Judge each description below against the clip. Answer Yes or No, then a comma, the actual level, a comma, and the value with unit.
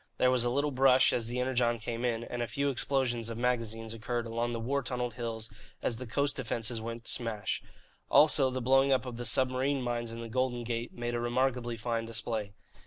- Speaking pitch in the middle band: No, low, 120 Hz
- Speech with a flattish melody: Yes, narrow, 1.8 semitones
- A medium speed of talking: No, fast, 215 wpm